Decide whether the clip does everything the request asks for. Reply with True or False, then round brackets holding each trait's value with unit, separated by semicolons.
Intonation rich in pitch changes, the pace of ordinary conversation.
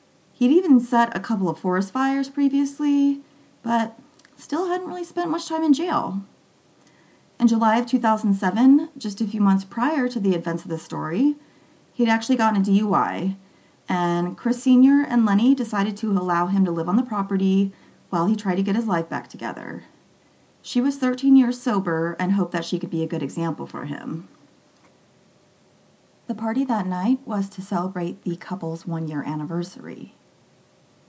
True (6.2 semitones; 170 wpm)